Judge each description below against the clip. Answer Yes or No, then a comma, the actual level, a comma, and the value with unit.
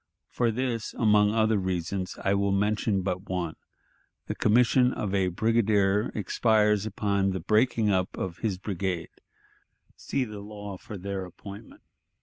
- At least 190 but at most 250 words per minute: No, average, 140 wpm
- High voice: No, low, 100 Hz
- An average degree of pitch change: No, narrow, 2.3 semitones